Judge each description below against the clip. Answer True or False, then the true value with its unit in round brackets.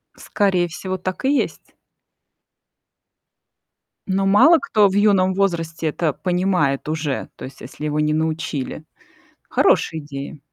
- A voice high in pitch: False (170 Hz)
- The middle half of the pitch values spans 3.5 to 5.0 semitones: True (4.1 semitones)